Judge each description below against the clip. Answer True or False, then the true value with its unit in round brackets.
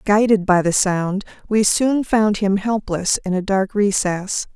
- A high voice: True (200 Hz)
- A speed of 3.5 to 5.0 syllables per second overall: True (3.9 syllables/s)